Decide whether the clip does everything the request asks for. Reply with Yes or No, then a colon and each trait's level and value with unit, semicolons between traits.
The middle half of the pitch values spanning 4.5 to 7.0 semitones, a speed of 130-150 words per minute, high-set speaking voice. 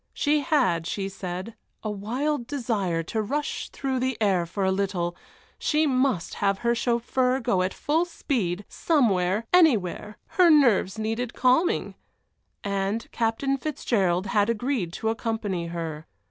Yes: wide, 5.5 semitones; average, 140 wpm; high, 225 Hz